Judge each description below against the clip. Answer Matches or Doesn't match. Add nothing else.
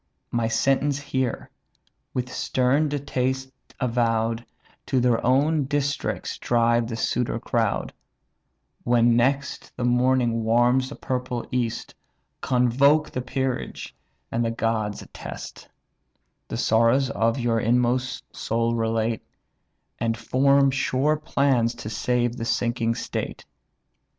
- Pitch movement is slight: Matches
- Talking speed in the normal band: Doesn't match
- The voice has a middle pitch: Doesn't match